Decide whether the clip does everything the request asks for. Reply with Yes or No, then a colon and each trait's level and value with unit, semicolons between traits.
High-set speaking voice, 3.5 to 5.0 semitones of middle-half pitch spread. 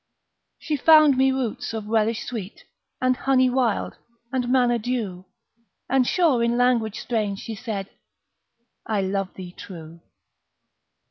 Yes: high, 235 Hz; average, 3.9 semitones